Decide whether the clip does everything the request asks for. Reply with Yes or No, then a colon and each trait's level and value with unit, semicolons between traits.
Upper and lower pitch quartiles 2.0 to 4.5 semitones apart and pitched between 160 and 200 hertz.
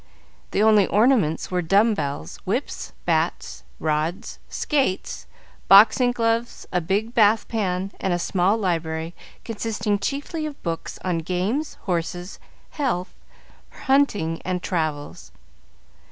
No: average, 5.2 semitones; high, 190 Hz